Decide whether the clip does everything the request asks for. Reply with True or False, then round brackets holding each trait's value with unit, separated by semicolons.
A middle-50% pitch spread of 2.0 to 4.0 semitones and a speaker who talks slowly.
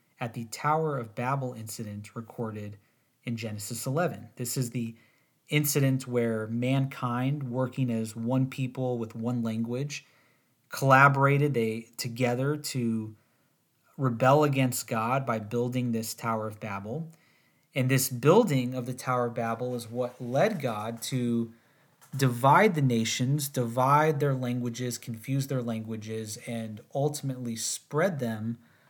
True (2.9 semitones; 130 wpm)